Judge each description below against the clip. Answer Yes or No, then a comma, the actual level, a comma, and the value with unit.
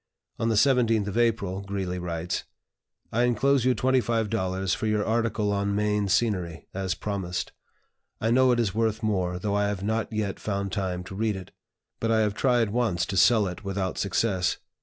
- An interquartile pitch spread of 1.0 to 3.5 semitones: Yes, average, 3.1 semitones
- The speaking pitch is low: Yes, low, 105 Hz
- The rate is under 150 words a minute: No, average, 180 wpm